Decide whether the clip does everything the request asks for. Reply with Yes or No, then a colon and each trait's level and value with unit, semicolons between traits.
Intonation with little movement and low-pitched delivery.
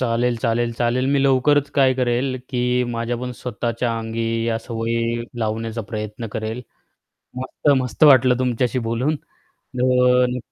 Yes: narrow, 1.8 semitones; low, 120 Hz